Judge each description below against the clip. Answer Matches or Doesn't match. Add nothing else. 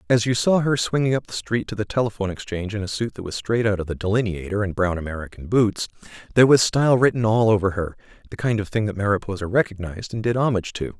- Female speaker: Doesn't match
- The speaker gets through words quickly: Matches